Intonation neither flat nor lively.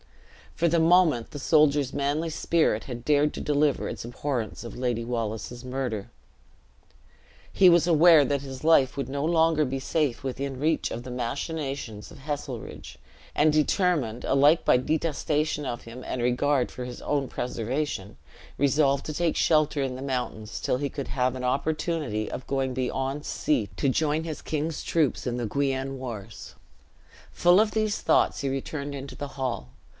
Yes: average, 3.4 semitones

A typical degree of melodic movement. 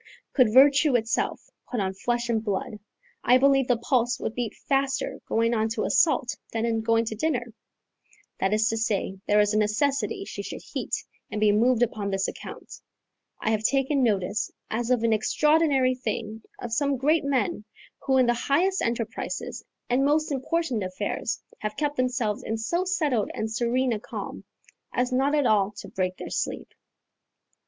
Yes: average, 3.9 semitones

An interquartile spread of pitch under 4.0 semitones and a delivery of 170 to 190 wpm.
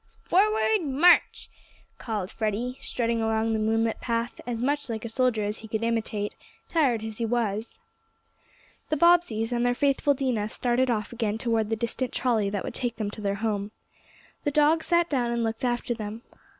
Yes: average, 2.8 semitones; average, 180 wpm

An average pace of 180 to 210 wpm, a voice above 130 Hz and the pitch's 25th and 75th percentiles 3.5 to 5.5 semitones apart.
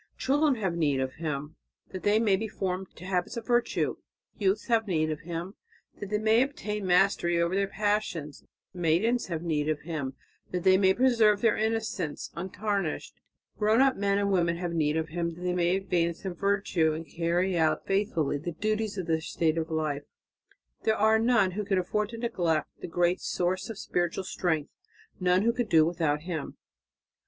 Yes: average, 185 wpm; medium, 185 Hz; average, 4.2 semitones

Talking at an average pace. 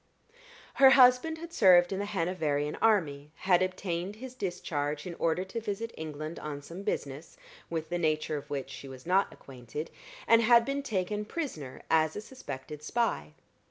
Yes: average, 165 wpm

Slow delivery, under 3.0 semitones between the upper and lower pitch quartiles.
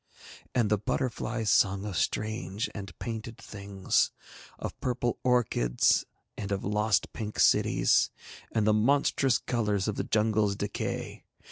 Yes: slow, 130 wpm; narrow, 2.4 semitones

